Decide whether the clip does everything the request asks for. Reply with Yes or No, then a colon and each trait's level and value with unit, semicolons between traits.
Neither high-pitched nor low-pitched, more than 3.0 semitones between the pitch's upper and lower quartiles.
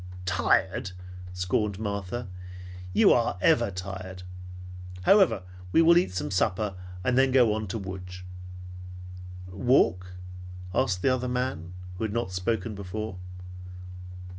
No: low, 100 Hz; average, 4.6 semitones